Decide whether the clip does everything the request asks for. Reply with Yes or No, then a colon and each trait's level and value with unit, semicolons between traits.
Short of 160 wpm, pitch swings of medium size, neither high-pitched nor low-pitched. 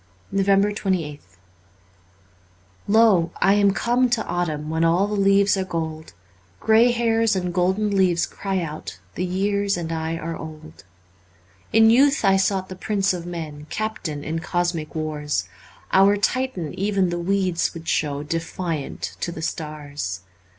Yes: average, 150 wpm; average, 3.9 semitones; medium, 180 Hz